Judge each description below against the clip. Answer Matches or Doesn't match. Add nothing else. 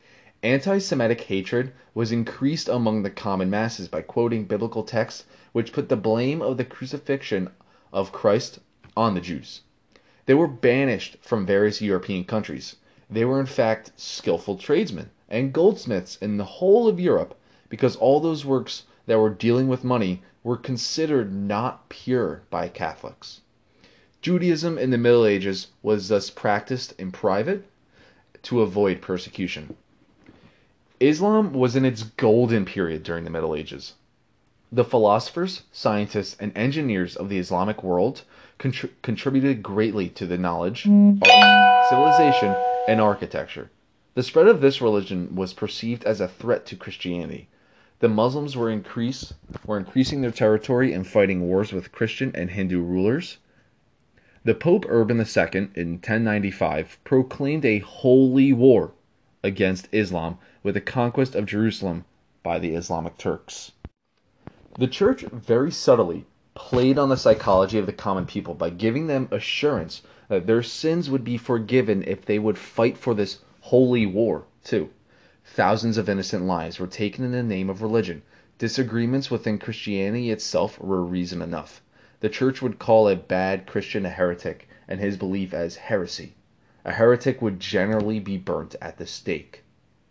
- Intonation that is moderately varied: Matches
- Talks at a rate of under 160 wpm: Matches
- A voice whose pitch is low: Matches